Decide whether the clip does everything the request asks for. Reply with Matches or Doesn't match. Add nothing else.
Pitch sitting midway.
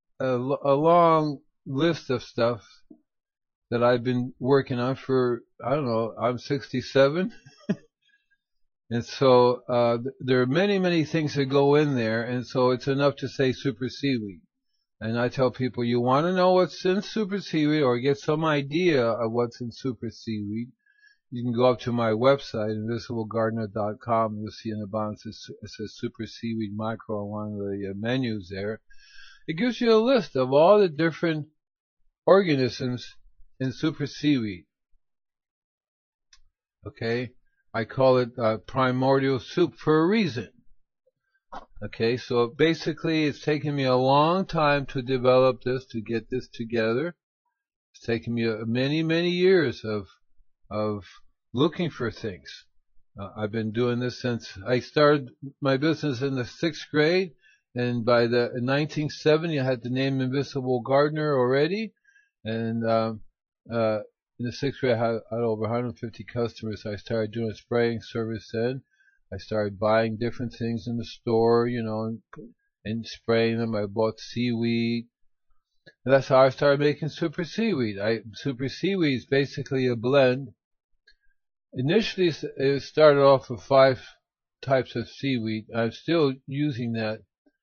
Doesn't match